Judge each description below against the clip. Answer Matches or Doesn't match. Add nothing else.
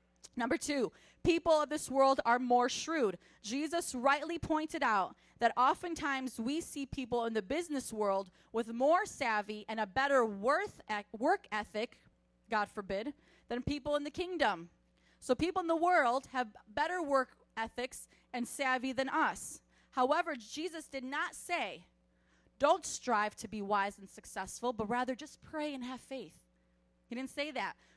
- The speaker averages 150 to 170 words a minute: Matches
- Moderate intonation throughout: Doesn't match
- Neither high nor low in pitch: Doesn't match